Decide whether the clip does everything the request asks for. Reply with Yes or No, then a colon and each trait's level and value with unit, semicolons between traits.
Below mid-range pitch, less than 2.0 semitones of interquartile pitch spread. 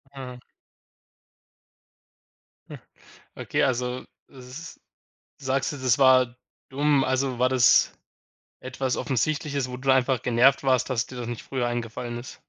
Yes: low, 130 Hz; narrow, 1.5 semitones